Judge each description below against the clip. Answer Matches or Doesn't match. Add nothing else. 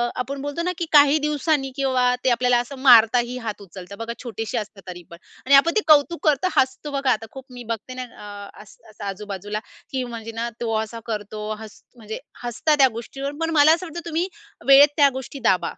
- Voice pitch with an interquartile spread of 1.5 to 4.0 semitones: Doesn't match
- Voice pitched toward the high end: Matches